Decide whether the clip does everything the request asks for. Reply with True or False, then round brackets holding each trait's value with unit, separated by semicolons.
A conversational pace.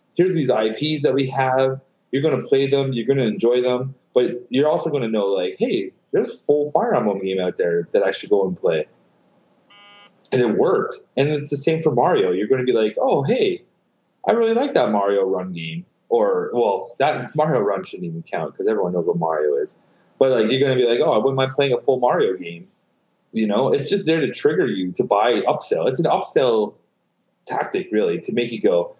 False (230 wpm)